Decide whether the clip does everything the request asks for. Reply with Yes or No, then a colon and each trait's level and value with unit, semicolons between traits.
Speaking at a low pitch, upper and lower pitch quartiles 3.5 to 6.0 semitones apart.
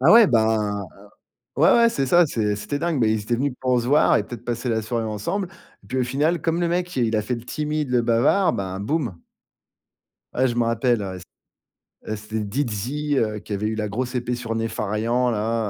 Yes: low, 120 Hz; average, 4.6 semitones